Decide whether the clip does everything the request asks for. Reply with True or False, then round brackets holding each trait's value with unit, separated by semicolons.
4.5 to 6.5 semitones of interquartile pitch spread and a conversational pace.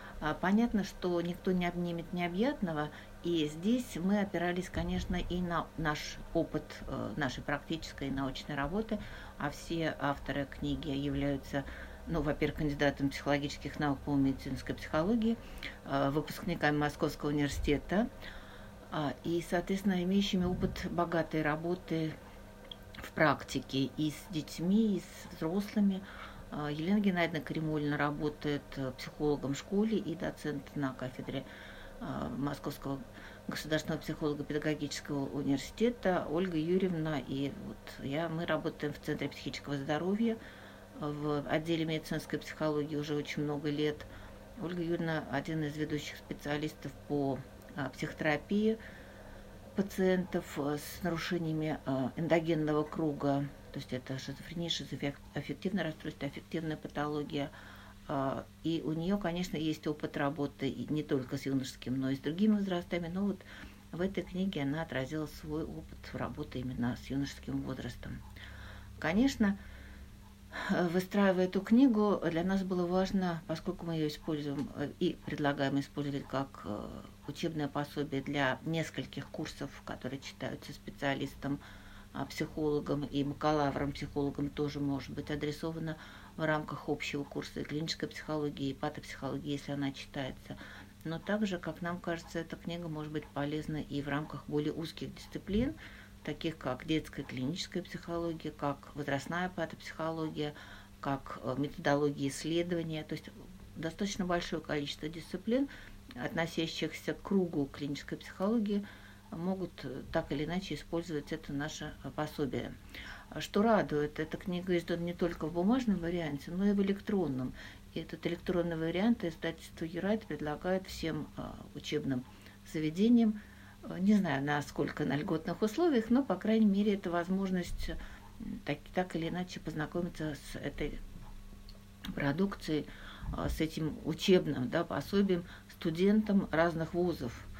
False (3.6 semitones; 120 wpm)